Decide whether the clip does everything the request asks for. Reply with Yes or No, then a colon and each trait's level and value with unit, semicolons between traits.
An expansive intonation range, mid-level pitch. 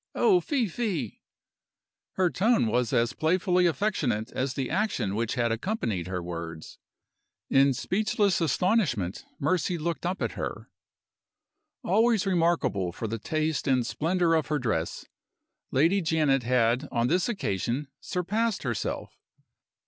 Yes: wide, 7.9 semitones; medium, 150 Hz